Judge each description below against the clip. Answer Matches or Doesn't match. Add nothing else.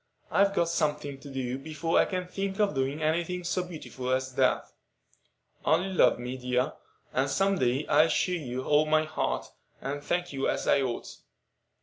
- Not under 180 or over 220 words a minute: Matches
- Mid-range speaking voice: Matches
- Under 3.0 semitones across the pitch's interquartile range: Doesn't match